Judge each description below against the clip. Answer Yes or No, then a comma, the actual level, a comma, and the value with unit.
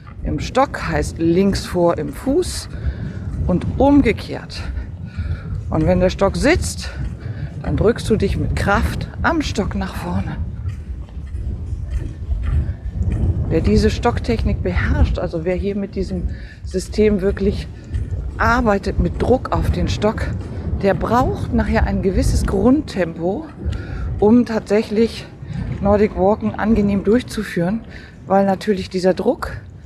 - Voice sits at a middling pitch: No, low, 125 Hz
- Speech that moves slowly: Yes, slow, 115 wpm